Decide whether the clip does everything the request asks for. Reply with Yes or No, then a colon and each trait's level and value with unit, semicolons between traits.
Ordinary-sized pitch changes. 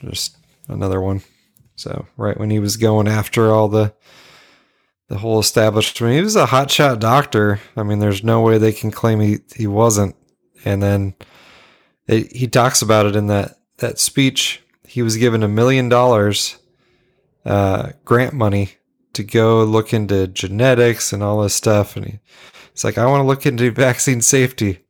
Yes: average, 3.0 semitones